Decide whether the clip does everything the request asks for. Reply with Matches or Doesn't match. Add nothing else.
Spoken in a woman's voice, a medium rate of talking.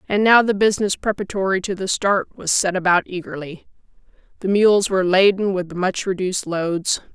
Matches